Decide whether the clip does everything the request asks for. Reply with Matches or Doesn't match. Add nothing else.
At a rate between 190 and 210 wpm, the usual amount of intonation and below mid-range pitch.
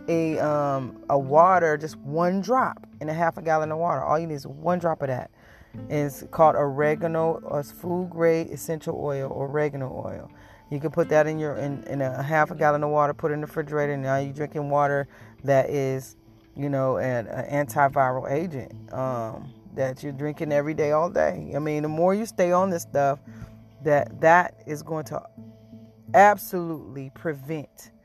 Doesn't match